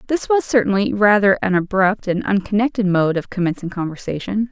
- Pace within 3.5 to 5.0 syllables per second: No, 5.6 syllables/s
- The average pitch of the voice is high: Yes, high, 200 Hz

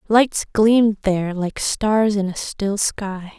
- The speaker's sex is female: Yes, female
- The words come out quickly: No, average, 160 wpm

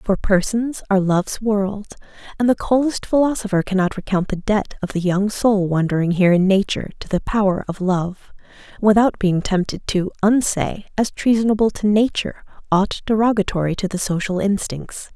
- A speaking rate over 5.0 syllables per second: Yes, 5.3 syllables/s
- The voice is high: Yes, high, 200 Hz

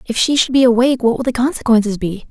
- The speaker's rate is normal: No, fast, 260 wpm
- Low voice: No, high, 240 Hz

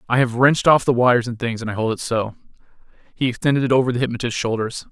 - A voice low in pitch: Yes, low, 120 Hz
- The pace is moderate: No, fast, 245 wpm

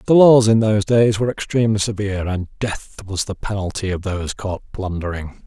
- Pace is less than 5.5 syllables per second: No, 5.8 syllables/s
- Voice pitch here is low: Yes, low, 100 Hz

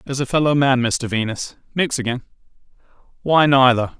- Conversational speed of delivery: No, slow, 120 wpm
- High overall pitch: No, low, 130 Hz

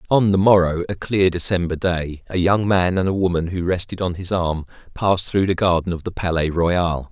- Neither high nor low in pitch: No, very low, 90 Hz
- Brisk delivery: Yes, fast, 220 wpm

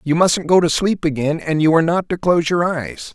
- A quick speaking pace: Yes, fast, 265 wpm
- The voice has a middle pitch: Yes, medium, 165 Hz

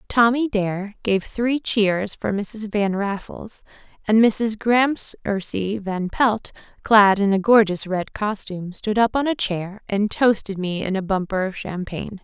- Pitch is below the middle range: No, high, 205 Hz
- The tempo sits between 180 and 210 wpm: No, average, 160 wpm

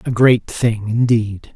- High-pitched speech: No, low, 115 Hz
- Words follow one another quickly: No, average, 155 wpm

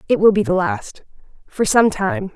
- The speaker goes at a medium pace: Yes, average, 180 wpm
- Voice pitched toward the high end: Yes, high, 205 Hz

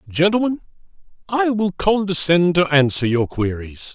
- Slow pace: Yes, slow, 120 wpm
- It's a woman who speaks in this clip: No, male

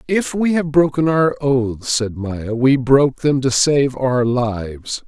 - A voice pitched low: Yes, low, 130 Hz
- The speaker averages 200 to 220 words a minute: No, average, 175 wpm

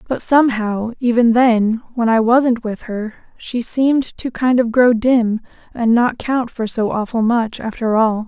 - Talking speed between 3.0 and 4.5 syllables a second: Yes, 4.2 syllables/s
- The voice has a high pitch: Yes, high, 235 Hz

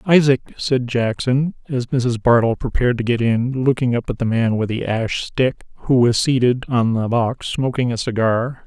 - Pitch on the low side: Yes, low, 125 Hz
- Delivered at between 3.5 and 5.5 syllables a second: Yes, 4.8 syllables/s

